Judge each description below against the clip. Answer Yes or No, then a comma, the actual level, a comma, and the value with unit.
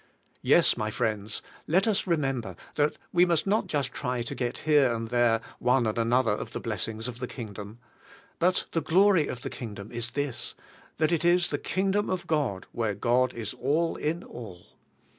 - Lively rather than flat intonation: Yes, wide, 6.2 semitones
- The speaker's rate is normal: Yes, average, 185 wpm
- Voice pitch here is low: Yes, low, 125 Hz